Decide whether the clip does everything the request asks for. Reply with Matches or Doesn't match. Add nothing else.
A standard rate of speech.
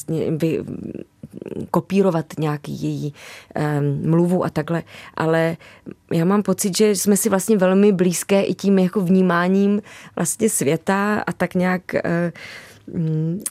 Matches